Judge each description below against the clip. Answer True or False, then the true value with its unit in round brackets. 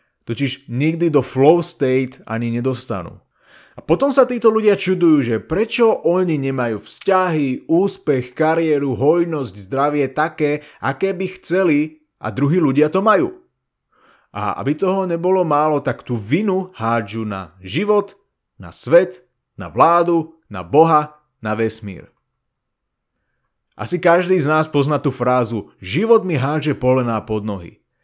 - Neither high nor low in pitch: True (150 Hz)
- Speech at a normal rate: True (135 wpm)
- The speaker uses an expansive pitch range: True (6.0 semitones)